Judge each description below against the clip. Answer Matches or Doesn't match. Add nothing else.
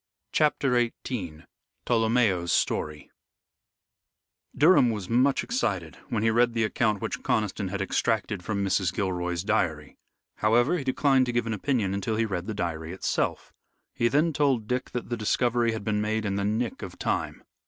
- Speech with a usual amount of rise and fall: Matches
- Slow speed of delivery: Doesn't match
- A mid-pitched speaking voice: Doesn't match